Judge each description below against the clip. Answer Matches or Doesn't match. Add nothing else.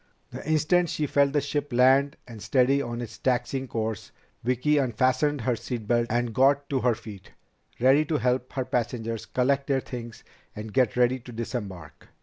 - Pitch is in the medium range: Doesn't match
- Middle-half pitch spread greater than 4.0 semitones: Doesn't match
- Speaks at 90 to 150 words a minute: Doesn't match